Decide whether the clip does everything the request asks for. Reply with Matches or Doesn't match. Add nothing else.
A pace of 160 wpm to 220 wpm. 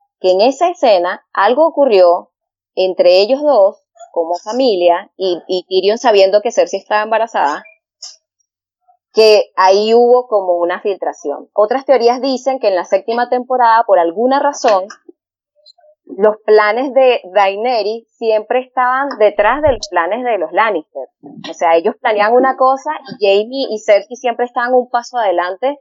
Doesn't match